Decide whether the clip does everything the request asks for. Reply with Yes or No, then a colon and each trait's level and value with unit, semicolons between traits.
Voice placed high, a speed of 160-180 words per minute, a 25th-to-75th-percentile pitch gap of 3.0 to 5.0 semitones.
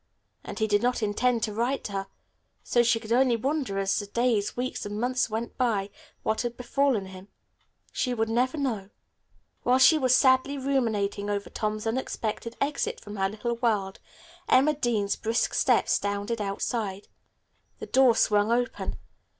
Yes: high, 230 Hz; average, 165 wpm; average, 3.5 semitones